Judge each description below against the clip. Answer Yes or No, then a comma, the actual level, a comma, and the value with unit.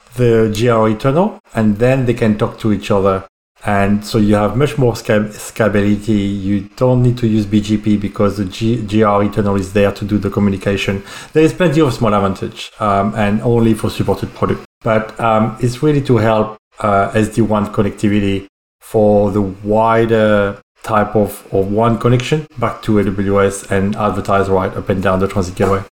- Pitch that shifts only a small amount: Yes, narrow, 2.2 semitones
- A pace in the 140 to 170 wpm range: No, average, 180 wpm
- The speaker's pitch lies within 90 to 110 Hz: Yes, low, 105 Hz